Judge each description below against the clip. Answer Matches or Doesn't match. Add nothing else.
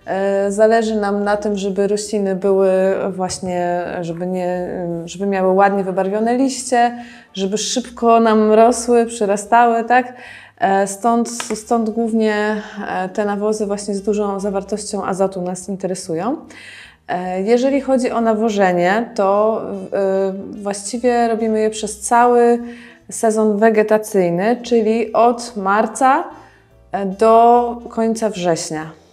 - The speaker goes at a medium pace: Doesn't match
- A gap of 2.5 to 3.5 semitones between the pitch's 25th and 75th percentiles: Matches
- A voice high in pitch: Matches